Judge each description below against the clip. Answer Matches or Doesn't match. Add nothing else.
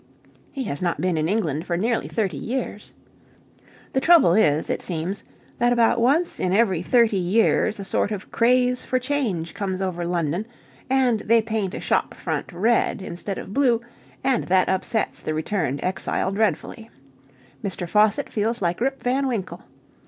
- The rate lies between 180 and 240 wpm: Doesn't match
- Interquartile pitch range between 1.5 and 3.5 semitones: Doesn't match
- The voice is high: Matches